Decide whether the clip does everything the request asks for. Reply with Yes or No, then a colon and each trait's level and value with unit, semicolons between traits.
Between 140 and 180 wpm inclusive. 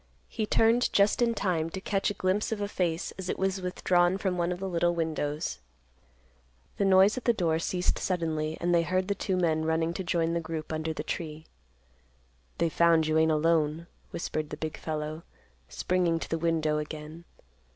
No: average, 195 wpm